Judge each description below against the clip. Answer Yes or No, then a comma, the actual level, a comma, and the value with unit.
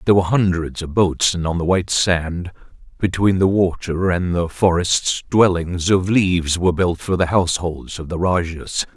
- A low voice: Yes, very low, 90 Hz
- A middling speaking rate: Yes, average, 180 wpm